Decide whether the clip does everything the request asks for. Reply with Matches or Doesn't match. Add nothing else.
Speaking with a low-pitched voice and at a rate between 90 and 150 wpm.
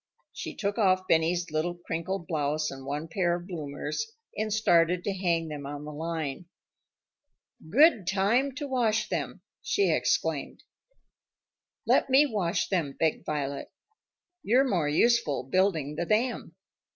Doesn't match